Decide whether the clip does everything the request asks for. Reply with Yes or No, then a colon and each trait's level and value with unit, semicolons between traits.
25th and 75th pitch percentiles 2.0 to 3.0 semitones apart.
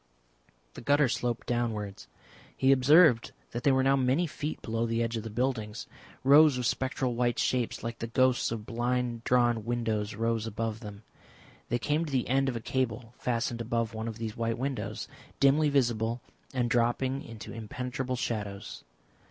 Yes: narrow, 2.4 semitones